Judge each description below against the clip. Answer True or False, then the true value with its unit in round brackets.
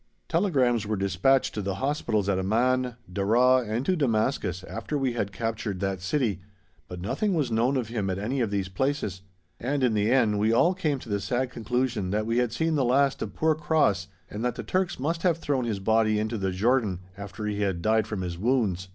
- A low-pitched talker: True (115 Hz)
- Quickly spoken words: True (215 wpm)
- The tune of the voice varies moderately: True (4.6 semitones)